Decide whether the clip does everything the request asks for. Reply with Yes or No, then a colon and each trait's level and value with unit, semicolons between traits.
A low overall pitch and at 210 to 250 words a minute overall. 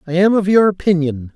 No: medium, 175 Hz; fast, 220 wpm